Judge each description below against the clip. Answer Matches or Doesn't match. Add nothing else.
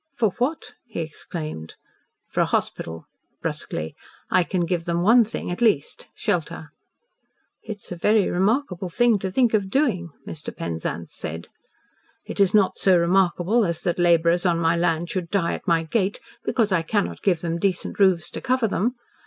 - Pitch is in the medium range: Matches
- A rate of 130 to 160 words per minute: Doesn't match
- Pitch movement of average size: Matches